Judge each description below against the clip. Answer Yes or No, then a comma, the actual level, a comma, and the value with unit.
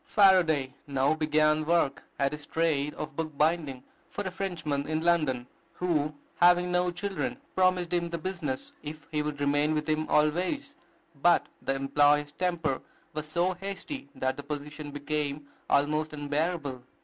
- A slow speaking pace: No, average, 150 wpm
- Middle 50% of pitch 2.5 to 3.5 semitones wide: Yes, average, 3.2 semitones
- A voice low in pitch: No, medium, 155 Hz